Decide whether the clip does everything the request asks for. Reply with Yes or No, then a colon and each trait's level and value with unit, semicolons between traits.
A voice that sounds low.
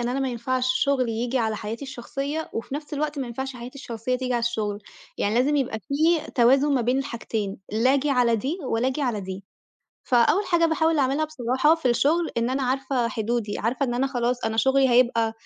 No: very high, 255 Hz